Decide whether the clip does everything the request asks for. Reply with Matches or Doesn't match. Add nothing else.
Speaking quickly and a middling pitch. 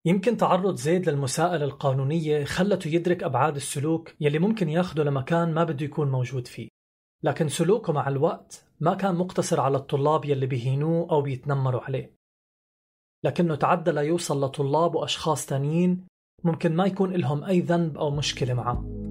Matches